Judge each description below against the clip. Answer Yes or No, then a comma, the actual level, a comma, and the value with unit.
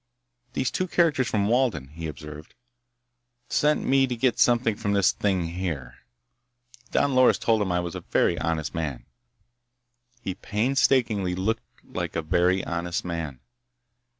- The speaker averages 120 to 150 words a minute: Yes, average, 145 wpm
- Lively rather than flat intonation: Yes, wide, 6.5 semitones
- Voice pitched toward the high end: No, very low, 95 Hz